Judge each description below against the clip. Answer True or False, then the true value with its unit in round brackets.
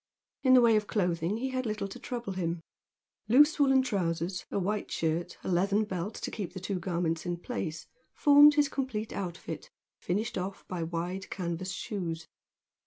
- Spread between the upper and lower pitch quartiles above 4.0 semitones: True (4.9 semitones)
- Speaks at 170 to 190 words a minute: True (175 wpm)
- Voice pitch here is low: False (195 Hz)